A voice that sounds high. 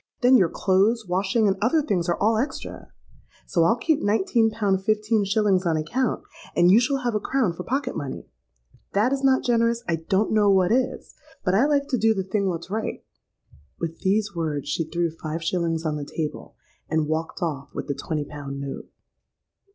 Yes: high, 195 Hz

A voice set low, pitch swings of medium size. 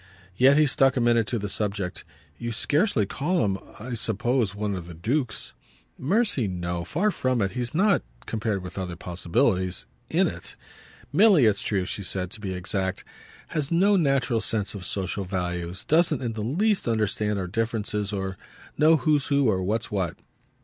No: low, 110 Hz; wide, 6.1 semitones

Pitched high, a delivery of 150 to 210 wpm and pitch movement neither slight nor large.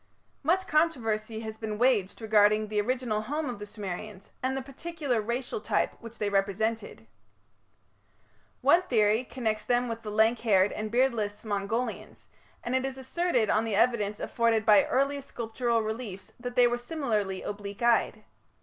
Yes: high, 225 Hz; average, 160 wpm; average, 3.0 semitones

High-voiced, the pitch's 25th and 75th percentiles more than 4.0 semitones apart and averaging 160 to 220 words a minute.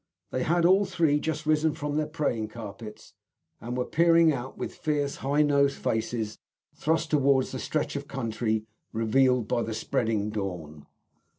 No: low, 135 Hz; wide, 5.5 semitones; average, 165 wpm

